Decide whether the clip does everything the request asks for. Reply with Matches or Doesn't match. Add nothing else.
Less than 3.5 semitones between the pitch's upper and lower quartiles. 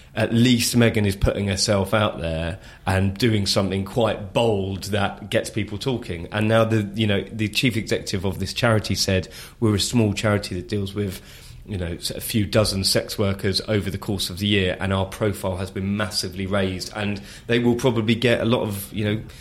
Matches